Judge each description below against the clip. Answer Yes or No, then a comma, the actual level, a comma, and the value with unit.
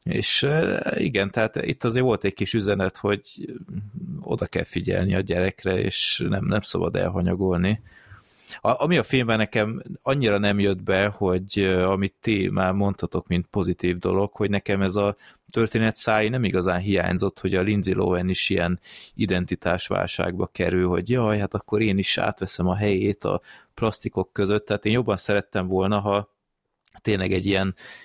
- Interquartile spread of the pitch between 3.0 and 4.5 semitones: No, narrow, 2.5 semitones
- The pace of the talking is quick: Yes, fast, 160 wpm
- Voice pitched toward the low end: Yes, low, 100 Hz